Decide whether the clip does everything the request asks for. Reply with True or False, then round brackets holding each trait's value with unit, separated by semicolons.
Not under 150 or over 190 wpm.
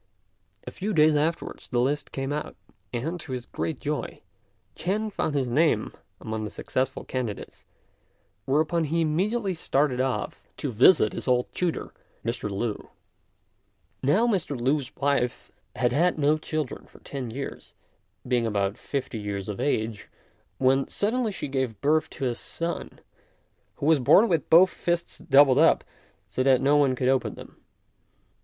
True (155 wpm)